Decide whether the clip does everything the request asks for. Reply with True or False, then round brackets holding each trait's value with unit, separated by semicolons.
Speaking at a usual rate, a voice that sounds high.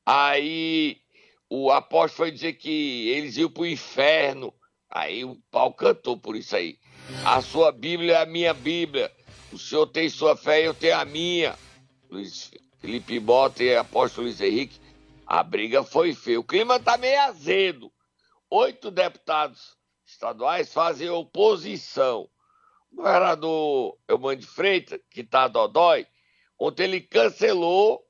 True (155 wpm; 325 Hz)